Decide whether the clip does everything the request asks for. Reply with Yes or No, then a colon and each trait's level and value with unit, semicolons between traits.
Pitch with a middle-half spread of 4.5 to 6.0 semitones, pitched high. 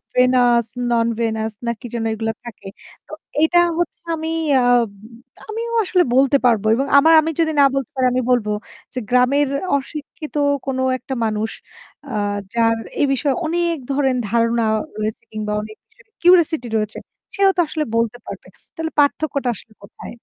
Yes: average, 5.3 semitones; very high, 255 Hz